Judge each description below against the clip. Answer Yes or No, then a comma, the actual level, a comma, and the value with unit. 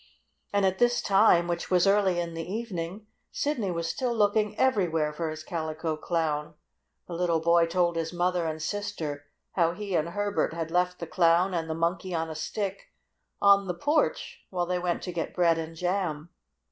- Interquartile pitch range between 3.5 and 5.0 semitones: No, average, 3.1 semitones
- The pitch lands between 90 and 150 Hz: No, medium, 175 Hz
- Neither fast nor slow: Yes, average, 185 wpm